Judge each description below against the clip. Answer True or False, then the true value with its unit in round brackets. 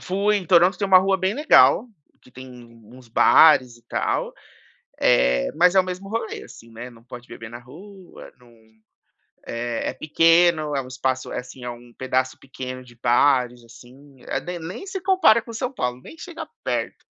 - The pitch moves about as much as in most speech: False (7.3 semitones)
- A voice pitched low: True (130 Hz)